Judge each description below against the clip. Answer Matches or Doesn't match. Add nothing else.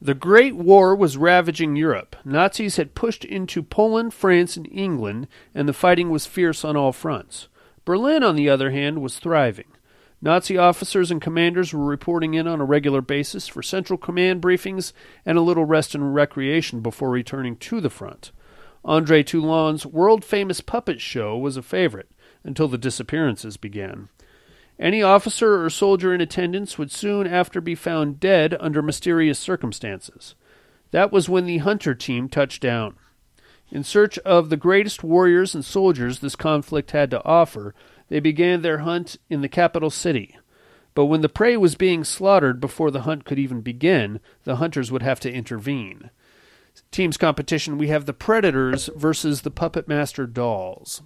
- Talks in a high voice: Doesn't match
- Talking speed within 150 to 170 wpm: Matches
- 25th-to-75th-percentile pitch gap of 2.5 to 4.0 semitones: Doesn't match